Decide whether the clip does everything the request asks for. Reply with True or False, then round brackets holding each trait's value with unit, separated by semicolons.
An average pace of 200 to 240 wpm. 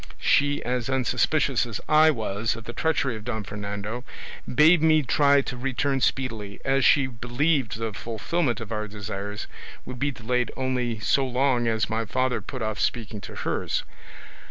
False (165 wpm)